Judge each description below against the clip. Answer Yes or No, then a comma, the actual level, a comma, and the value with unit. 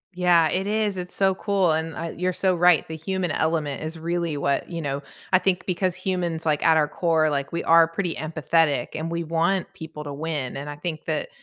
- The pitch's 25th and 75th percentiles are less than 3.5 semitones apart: Yes, narrow, 2.5 semitones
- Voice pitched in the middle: Yes, medium, 165 Hz